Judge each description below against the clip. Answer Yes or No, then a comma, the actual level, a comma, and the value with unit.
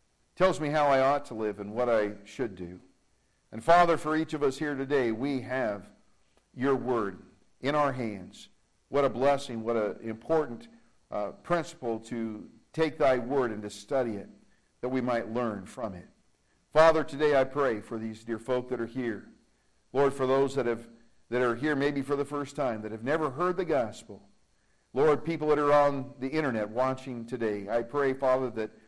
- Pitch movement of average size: Yes, average, 4.1 semitones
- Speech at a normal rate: Yes, average, 190 wpm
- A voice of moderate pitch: No, low, 130 Hz